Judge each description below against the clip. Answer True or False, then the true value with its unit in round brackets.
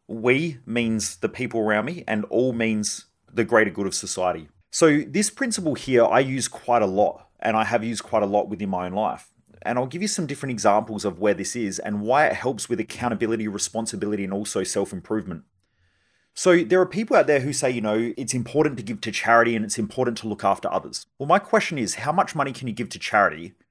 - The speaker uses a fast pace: True (230 wpm)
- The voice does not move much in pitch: False (3.6 semitones)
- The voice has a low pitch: True (115 Hz)